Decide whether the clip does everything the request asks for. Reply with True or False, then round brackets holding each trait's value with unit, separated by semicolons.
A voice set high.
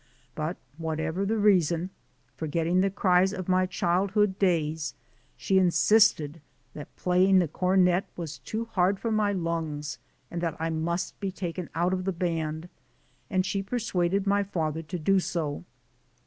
False (180 Hz)